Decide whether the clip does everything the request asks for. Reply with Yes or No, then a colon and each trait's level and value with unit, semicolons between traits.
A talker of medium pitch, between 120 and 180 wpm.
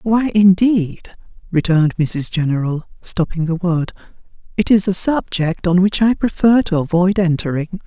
Yes: medium, 180 Hz; average, 145 wpm